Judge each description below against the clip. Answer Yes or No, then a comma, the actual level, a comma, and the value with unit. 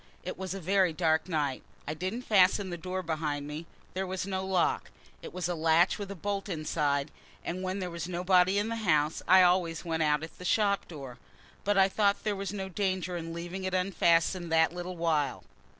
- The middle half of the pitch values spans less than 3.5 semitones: Yes, average, 2.8 semitones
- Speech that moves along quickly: Yes, fast, 210 wpm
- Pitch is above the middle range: No, medium, 180 Hz